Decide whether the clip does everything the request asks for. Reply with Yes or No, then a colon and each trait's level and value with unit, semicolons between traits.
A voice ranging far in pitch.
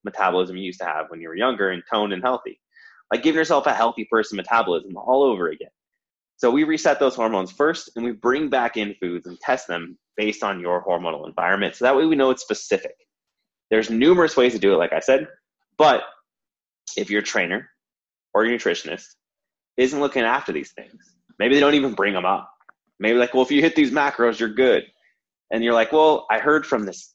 Yes: wide, 6.1 semitones